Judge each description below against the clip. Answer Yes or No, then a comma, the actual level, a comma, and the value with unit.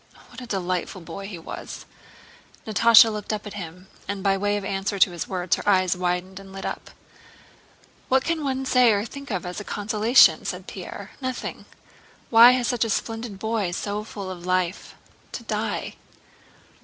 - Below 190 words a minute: Yes, average, 175 wpm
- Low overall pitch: No, high, 205 Hz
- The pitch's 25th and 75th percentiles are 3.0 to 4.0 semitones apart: Yes, average, 3.4 semitones